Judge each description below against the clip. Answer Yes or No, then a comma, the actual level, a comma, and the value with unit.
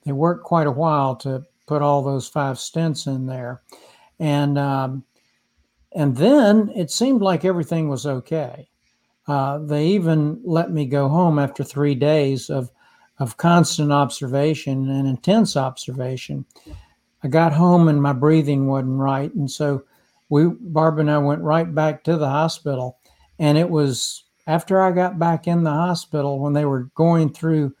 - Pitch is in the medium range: Yes, medium, 150 Hz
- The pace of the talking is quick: No, average, 160 wpm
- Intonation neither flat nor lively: Yes, average, 3.2 semitones